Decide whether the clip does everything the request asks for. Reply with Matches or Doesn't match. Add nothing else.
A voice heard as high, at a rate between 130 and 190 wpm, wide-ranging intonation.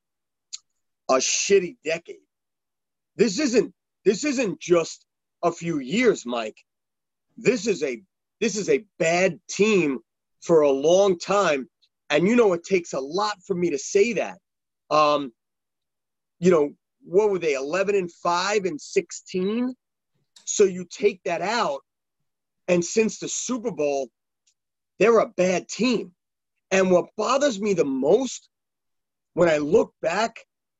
Matches